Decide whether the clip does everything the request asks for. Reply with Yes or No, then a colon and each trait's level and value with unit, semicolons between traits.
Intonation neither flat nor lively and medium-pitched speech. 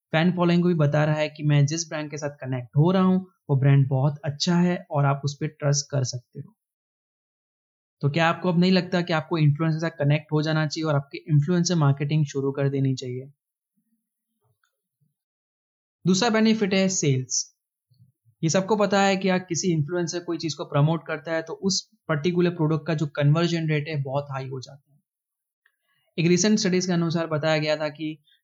Yes: average, 3.7 semitones; medium, 160 Hz